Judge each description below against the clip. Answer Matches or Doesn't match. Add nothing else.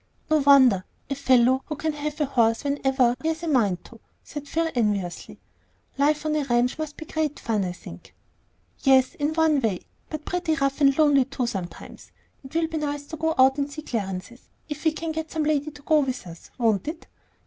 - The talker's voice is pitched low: Doesn't match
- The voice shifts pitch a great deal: Doesn't match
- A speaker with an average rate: Doesn't match